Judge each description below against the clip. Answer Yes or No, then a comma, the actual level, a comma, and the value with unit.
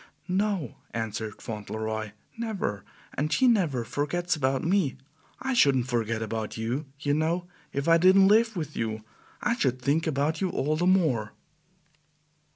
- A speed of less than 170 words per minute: Yes, average, 150 wpm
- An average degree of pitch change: No, wide, 7.8 semitones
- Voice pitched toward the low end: No, medium, 145 Hz